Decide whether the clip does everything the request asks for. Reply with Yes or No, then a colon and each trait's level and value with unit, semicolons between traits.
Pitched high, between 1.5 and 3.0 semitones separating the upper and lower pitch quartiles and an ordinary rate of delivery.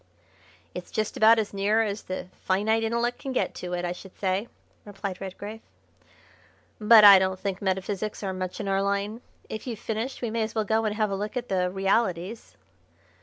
Yes: high, 205 Hz; narrow, 2.6 semitones; average, 195 wpm